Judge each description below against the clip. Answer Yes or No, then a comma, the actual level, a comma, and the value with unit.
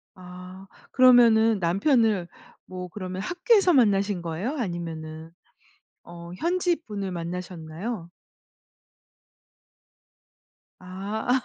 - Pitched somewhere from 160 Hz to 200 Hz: Yes, high, 190 Hz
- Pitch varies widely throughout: No, average, 4.8 semitones